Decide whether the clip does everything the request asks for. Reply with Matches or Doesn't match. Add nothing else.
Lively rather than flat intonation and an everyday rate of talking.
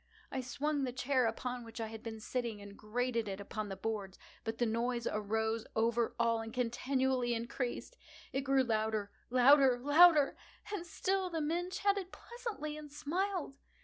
Doesn't match